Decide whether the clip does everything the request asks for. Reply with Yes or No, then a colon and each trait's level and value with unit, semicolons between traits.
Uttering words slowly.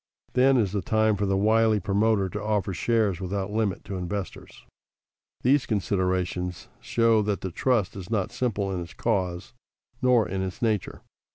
No: average, 165 wpm